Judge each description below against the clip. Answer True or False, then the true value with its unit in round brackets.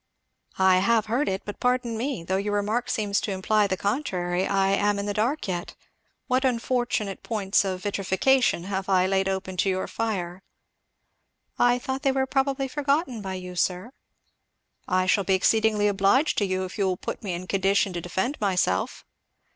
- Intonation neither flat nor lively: True (4.1 semitones)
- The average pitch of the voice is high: True (200 Hz)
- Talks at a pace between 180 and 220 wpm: True (185 wpm)